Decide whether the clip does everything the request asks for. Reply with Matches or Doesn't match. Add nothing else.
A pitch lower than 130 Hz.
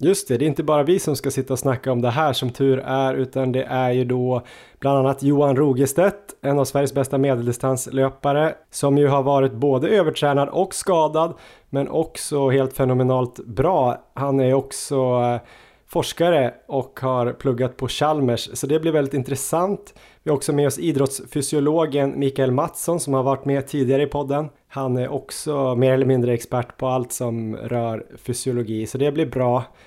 Doesn't match